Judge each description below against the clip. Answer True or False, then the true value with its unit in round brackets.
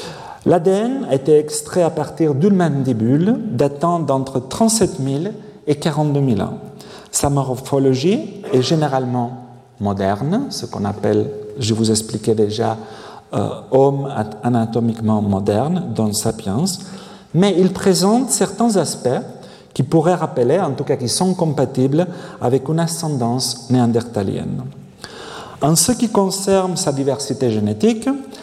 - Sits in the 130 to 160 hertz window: True (140 Hz)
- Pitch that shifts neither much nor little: False (7.4 semitones)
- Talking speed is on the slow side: True (125 wpm)